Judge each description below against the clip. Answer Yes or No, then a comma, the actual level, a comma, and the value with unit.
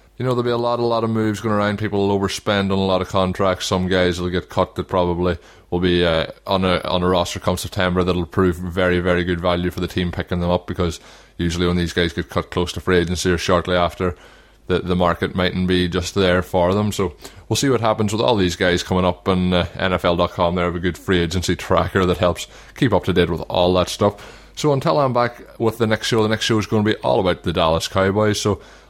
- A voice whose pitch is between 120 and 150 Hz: No, very low, 90 Hz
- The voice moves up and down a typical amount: No, narrow, 2.2 semitones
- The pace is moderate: No, fast, 255 wpm